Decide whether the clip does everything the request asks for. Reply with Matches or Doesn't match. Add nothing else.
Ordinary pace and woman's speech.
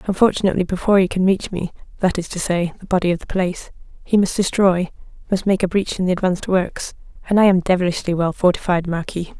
Doesn't match